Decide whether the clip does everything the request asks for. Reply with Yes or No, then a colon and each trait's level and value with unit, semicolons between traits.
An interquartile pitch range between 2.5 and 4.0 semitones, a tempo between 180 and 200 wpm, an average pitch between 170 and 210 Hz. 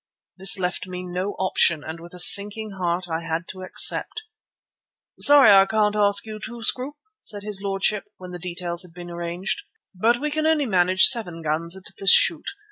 Yes: average, 3.2 semitones; average, 185 wpm; high, 190 Hz